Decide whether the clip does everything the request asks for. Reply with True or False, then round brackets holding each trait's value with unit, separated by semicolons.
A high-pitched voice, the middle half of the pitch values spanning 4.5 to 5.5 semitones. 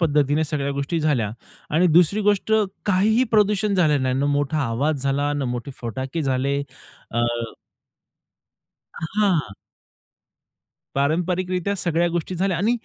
False (155 Hz; 4.9 semitones)